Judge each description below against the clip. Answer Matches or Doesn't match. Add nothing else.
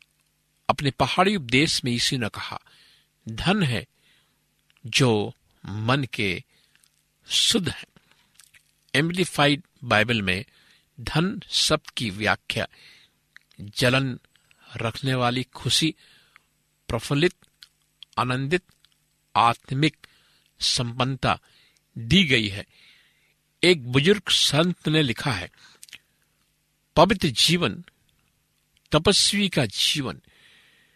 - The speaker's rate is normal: Doesn't match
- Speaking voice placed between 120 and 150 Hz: Matches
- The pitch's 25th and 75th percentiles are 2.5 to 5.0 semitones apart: Doesn't match